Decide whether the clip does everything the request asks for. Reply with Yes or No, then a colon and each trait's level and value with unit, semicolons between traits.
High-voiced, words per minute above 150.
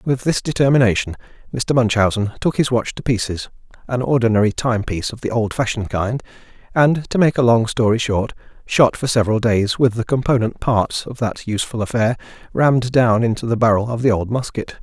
No: low, 115 Hz; average, 185 wpm